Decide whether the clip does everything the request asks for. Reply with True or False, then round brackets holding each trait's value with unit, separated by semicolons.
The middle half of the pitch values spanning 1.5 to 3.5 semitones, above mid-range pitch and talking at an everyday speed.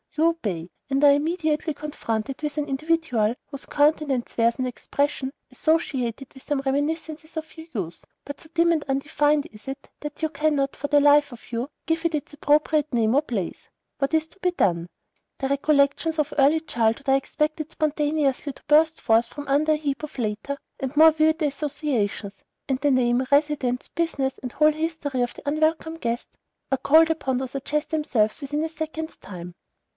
True (3.0 semitones; 290 Hz; 180 wpm)